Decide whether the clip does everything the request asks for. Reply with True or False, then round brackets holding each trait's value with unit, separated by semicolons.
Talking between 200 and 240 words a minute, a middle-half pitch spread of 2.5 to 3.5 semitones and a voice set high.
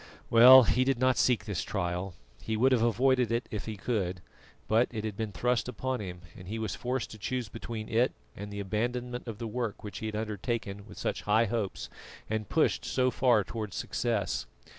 False (205 wpm; 3.0 semitones; 110 Hz)